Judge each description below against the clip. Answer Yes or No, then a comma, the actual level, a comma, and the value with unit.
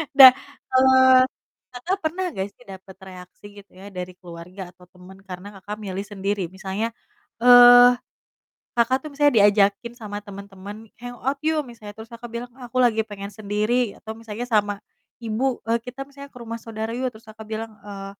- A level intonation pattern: No, average, 3.7 semitones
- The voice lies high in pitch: Yes, high, 220 Hz